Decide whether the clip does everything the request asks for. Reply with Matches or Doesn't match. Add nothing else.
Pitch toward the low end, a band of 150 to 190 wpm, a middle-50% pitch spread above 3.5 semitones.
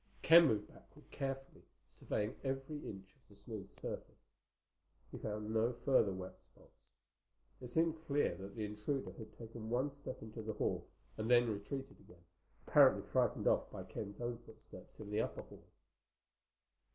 Matches